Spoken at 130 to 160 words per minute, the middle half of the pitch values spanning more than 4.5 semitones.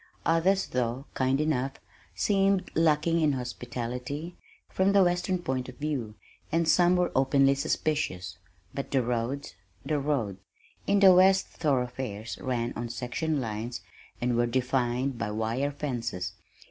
Yes: slow, 135 wpm; average, 5.0 semitones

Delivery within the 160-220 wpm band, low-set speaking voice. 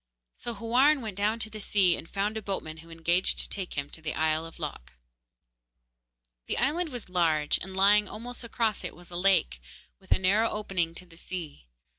No: average, 200 wpm; high, 190 Hz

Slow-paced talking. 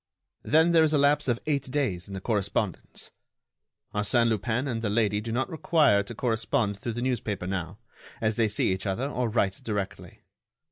No: average, 185 wpm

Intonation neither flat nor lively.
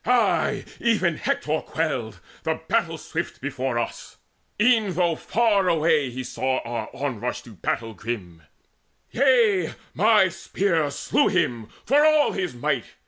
No: wide, 8.6 semitones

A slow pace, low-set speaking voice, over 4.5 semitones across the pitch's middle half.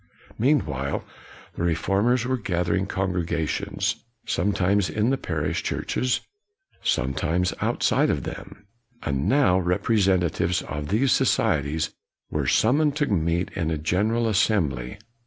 Yes: slow, 120 wpm; very low, 90 Hz; average, 5.3 semitones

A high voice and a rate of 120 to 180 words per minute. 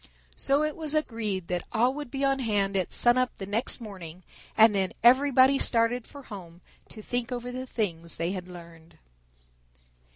Yes: high, 230 Hz; average, 175 wpm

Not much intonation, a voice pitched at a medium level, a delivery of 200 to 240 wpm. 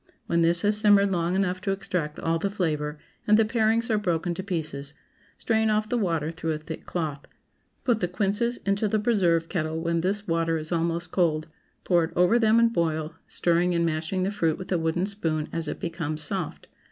No: average, 3.7 semitones; medium, 175 Hz; fast, 205 wpm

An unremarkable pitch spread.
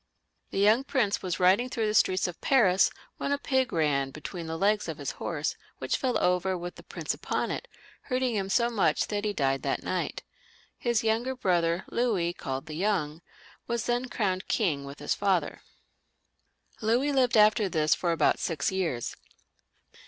No: wide, 5.9 semitones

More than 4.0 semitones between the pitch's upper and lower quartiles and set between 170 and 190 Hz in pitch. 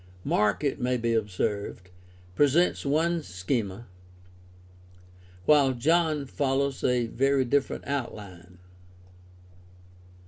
No: average, 5.1 semitones; low, 130 Hz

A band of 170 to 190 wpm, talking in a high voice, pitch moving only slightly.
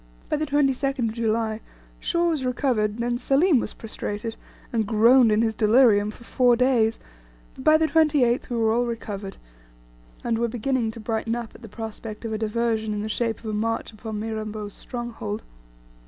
Yes: average, 180 wpm; high, 230 Hz; narrow, 2.3 semitones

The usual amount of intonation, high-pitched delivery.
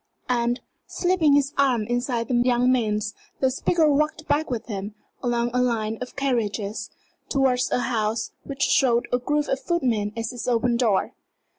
Yes: average, 3.1 semitones; high, 245 Hz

